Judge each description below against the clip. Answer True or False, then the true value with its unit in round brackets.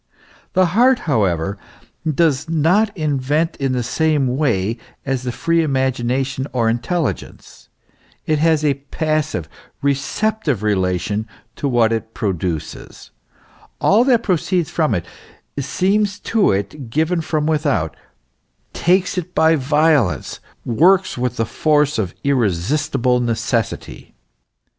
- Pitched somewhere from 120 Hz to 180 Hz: True (140 Hz)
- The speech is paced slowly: True (120 wpm)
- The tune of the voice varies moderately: False (5.8 semitones)